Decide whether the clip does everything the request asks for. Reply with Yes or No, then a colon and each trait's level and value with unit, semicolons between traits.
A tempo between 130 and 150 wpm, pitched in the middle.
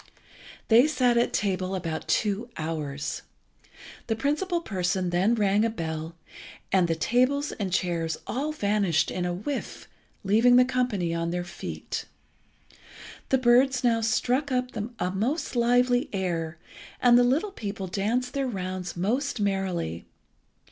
No: average, 140 wpm; high, 210 Hz